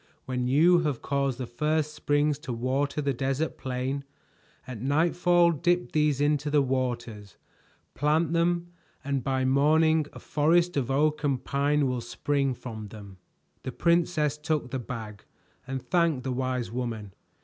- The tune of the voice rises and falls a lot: No, average, 3.3 semitones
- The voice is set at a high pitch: No, medium, 140 Hz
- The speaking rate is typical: Yes, average, 150 wpm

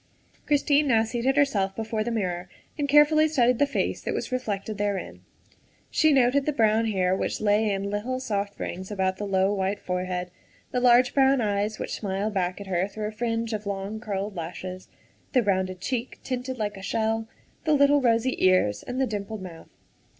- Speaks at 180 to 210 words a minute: Yes, average, 185 wpm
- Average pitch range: Yes, average, 4.4 semitones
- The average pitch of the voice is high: Yes, high, 215 Hz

